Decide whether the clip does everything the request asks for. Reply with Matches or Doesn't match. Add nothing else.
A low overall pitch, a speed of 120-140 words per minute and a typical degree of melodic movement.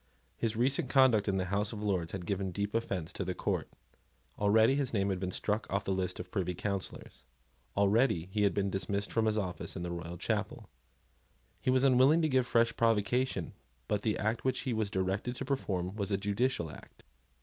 Doesn't match